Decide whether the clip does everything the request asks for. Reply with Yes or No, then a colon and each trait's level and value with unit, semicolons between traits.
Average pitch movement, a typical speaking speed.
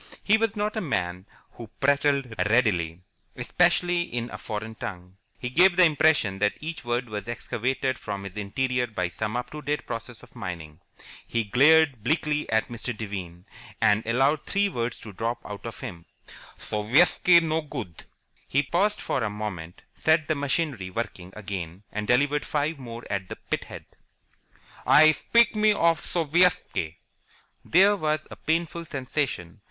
No: wide, 7.1 semitones; average, 160 wpm